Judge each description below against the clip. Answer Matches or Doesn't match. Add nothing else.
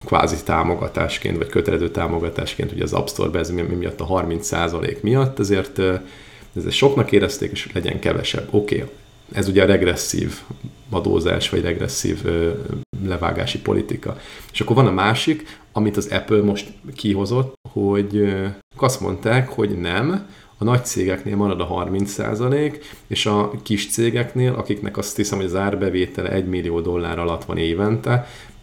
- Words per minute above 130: Matches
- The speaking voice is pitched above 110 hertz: Doesn't match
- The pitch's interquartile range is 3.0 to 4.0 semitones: Matches